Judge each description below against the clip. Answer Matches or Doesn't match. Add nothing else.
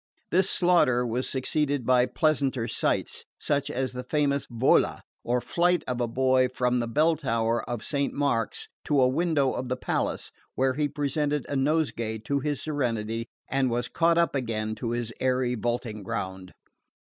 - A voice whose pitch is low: Matches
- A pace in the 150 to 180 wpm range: Matches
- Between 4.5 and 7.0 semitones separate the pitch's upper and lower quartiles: Doesn't match